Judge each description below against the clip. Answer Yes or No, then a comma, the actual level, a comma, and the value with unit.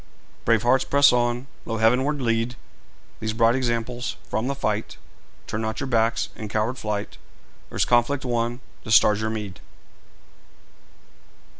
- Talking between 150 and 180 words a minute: No, average, 140 wpm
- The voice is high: No, low, 115 Hz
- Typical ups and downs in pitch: No, narrow, 2.1 semitones